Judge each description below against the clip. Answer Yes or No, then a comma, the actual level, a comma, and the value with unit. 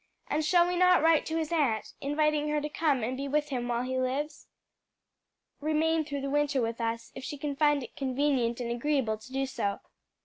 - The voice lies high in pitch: Yes, very high, 285 Hz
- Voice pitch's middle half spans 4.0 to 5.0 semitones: No, average, 3.2 semitones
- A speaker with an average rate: No, fast, 210 wpm